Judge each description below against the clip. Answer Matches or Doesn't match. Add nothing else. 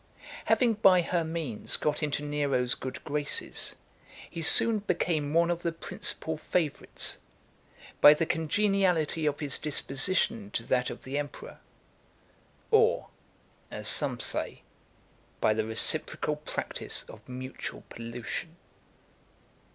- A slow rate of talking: Matches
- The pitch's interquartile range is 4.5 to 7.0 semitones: Doesn't match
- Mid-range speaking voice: Matches